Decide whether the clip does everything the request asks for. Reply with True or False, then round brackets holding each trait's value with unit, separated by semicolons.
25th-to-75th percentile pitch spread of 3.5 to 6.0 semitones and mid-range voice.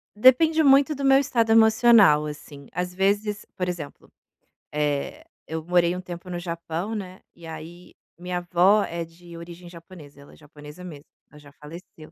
True (4.6 semitones; 175 Hz)